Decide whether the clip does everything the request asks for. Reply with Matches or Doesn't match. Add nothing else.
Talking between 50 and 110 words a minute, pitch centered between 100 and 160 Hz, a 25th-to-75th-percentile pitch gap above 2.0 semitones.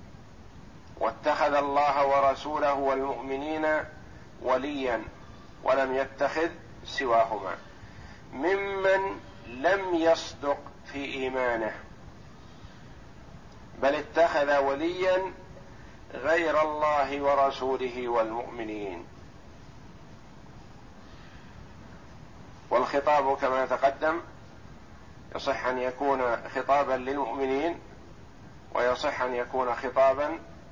Matches